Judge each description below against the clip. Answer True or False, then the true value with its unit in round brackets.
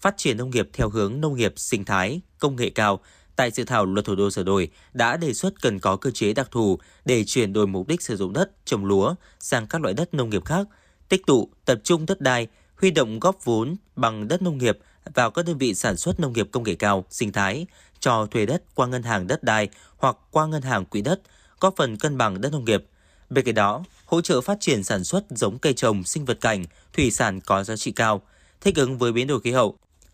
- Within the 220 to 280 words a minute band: True (245 wpm)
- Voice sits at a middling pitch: False (120 Hz)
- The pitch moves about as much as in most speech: False (7.4 semitones)